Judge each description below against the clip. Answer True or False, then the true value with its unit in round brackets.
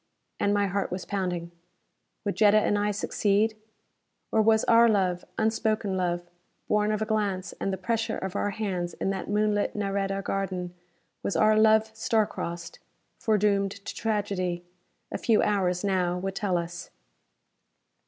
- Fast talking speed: False (155 wpm)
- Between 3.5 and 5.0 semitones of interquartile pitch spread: False (2.5 semitones)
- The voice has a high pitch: True (200 Hz)